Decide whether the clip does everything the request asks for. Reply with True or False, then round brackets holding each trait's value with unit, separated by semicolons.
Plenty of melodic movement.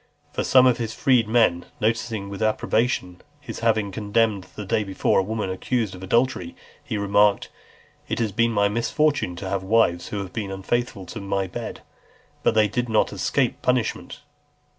False (3.0 semitones)